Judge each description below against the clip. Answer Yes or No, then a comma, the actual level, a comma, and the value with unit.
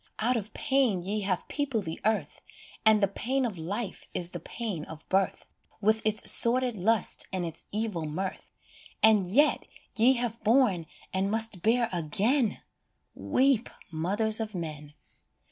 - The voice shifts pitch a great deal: No, average, 4.3 semitones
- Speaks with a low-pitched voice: No, high, 215 Hz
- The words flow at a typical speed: Yes, average, 155 wpm